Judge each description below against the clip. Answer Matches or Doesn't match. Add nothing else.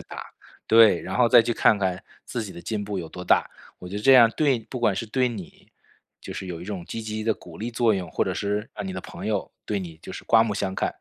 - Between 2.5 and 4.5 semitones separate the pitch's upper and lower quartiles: Matches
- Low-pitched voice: Matches